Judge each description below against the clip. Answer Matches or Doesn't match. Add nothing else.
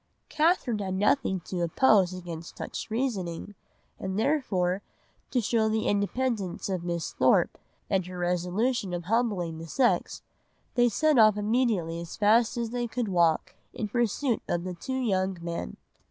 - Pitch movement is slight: Doesn't match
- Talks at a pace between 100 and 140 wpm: Doesn't match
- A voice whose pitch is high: Matches